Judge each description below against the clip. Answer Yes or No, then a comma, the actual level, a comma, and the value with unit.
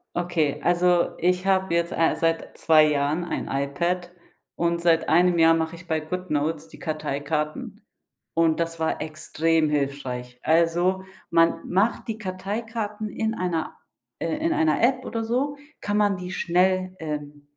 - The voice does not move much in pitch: No, average, 3.0 semitones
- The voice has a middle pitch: Yes, medium, 170 Hz